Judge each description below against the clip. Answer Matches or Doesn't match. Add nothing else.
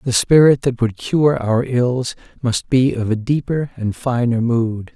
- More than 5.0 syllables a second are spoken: Doesn't match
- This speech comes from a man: Matches